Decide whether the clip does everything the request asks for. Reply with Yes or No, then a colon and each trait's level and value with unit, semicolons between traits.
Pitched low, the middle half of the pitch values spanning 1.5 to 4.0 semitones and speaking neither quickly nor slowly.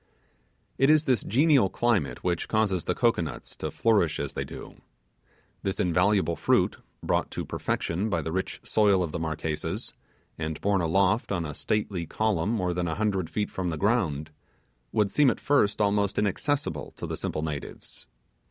No: very low, 95 Hz; average, 4.7 semitones; average, 170 wpm